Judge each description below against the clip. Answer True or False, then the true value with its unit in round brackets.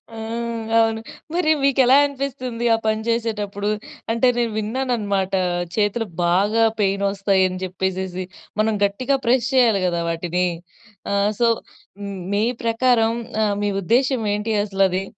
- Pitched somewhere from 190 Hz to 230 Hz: True (215 Hz)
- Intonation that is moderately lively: True (3.5 semitones)